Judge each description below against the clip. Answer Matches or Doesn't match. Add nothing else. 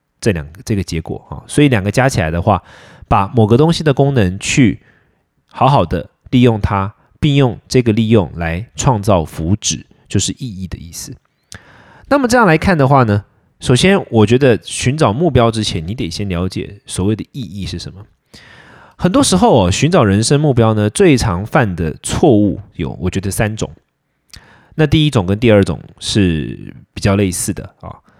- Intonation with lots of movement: Doesn't match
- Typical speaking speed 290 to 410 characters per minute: Doesn't match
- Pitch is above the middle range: Doesn't match